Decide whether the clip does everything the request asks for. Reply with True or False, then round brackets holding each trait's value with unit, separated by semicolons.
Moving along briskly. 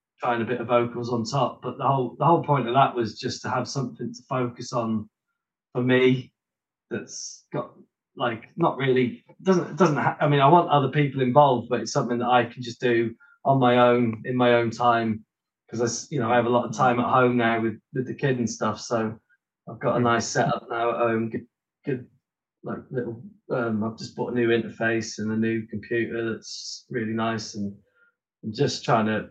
True (215 wpm)